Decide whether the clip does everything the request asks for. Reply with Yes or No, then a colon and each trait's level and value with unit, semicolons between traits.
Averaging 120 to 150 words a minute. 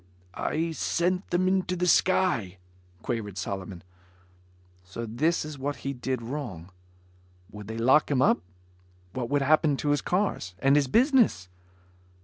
Yes: average, 140 wpm